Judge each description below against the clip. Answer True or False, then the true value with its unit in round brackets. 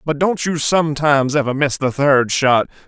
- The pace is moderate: True (190 wpm)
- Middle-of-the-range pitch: True (145 Hz)